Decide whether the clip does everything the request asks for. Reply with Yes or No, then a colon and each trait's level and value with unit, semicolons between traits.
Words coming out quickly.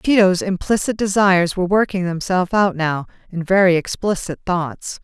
No: average, 145 wpm